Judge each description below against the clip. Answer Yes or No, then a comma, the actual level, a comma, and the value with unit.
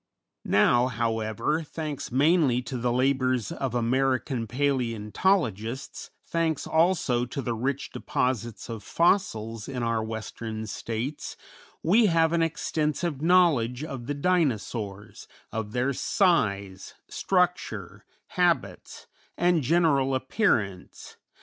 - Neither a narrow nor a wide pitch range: No, wide, 5.8 semitones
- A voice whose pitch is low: Yes, low, 130 Hz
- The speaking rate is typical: No, slow, 105 wpm